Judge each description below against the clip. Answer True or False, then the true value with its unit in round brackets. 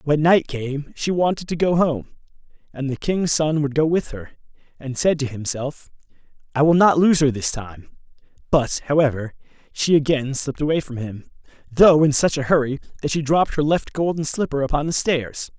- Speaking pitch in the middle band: True (145 Hz)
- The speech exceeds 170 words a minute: True (190 wpm)